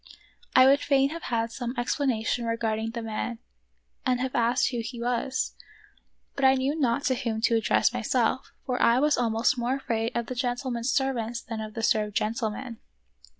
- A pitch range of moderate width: No, narrow, 2.3 semitones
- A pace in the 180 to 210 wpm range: Yes, average, 185 wpm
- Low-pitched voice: No, high, 240 Hz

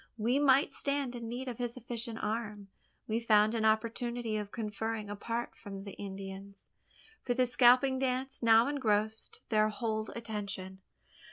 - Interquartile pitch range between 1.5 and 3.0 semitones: Yes, narrow, 2.6 semitones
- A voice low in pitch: No, high, 225 Hz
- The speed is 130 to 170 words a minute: Yes, average, 150 wpm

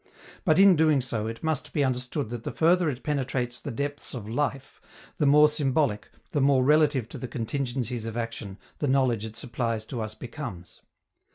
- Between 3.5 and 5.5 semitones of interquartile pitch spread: Yes, average, 4.2 semitones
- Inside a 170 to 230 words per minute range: Yes, average, 185 wpm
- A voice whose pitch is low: Yes, low, 130 Hz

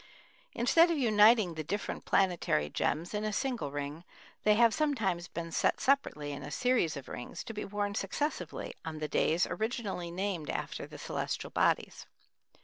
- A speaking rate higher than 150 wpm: Yes, average, 165 wpm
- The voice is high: Yes, high, 195 Hz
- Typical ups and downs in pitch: No, wide, 6.4 semitones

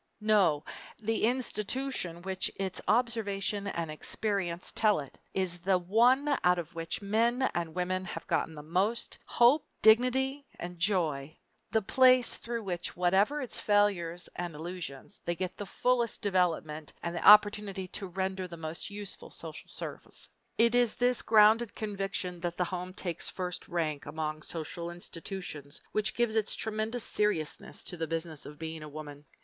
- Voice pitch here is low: No, medium, 185 Hz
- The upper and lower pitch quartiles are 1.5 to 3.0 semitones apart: No, average, 4.4 semitones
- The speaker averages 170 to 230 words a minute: No, average, 160 wpm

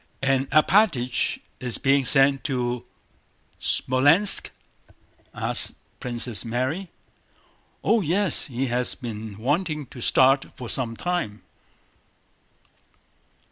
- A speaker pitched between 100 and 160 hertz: Yes, low, 135 Hz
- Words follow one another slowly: Yes, slow, 95 wpm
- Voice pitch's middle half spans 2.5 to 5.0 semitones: Yes, average, 3.9 semitones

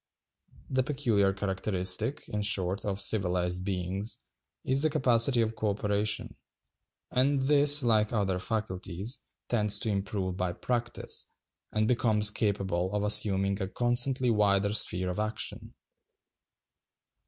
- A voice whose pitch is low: Yes, low, 105 Hz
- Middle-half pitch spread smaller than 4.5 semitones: Yes, average, 3.6 semitones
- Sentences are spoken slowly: Yes, slow, 120 wpm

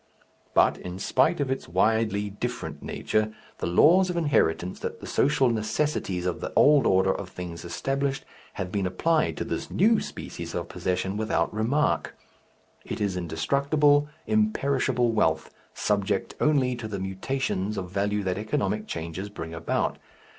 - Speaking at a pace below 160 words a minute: Yes, average, 150 wpm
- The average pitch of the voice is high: No, low, 105 Hz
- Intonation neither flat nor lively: No, wide, 6.7 semitones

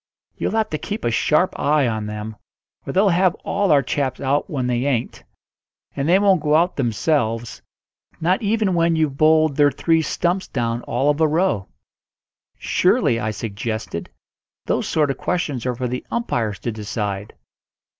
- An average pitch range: No, wide, 6.4 semitones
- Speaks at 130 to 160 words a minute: No, average, 170 wpm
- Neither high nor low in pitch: Yes, medium, 145 Hz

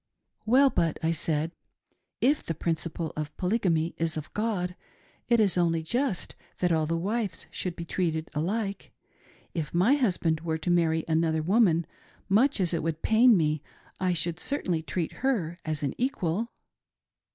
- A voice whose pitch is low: No, medium, 170 Hz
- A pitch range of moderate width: Yes, average, 4.6 semitones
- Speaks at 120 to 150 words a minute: No, average, 165 wpm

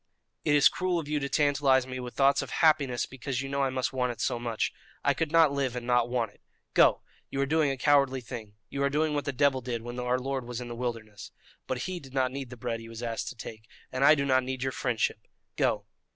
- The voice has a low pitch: Yes, low, 130 Hz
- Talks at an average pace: No, fast, 260 wpm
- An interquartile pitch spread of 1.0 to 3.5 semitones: Yes, narrow, 2.4 semitones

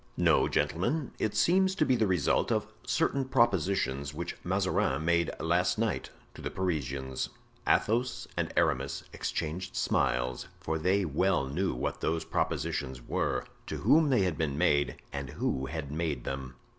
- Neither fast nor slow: Yes, average, 155 wpm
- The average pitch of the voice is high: No, very low, 85 Hz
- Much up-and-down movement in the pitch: Yes, wide, 6.3 semitones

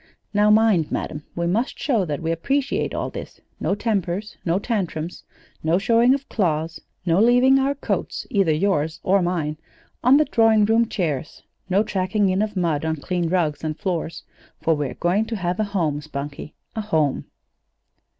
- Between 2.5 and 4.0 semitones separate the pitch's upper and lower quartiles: No, average, 5.1 semitones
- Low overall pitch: No, medium, 185 Hz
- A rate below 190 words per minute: Yes, average, 170 wpm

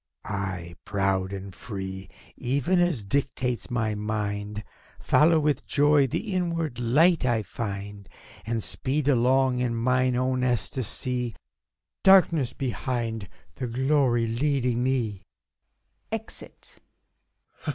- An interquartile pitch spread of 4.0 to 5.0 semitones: Yes, average, 4.7 semitones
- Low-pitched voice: Yes, low, 125 Hz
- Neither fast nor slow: No, slow, 105 wpm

